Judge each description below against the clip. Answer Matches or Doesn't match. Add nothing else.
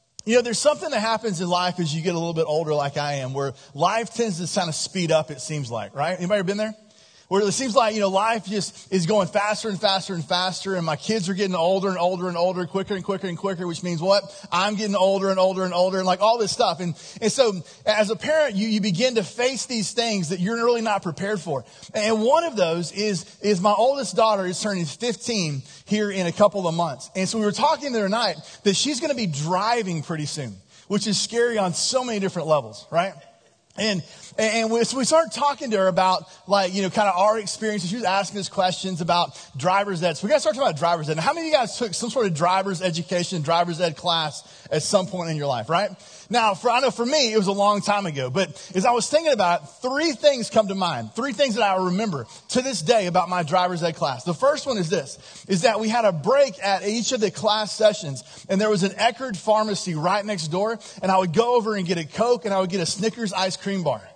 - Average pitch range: Matches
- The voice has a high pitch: Matches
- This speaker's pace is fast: Matches